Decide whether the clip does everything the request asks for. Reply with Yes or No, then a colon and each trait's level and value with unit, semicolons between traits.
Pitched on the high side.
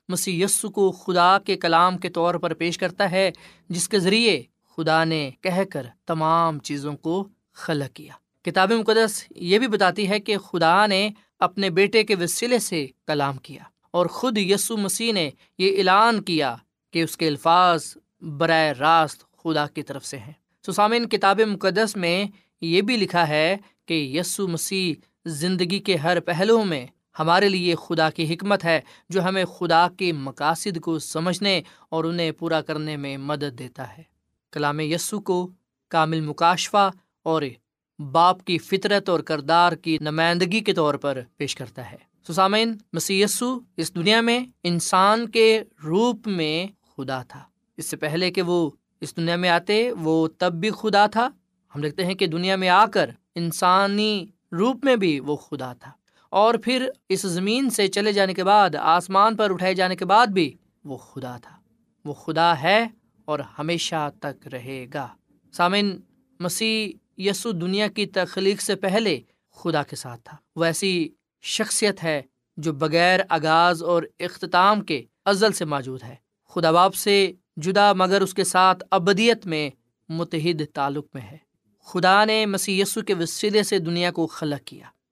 No: medium, 175 Hz